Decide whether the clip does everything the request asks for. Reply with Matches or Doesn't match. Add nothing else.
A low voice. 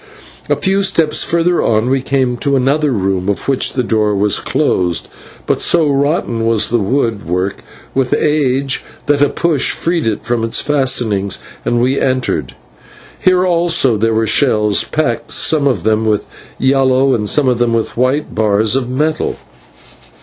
Matches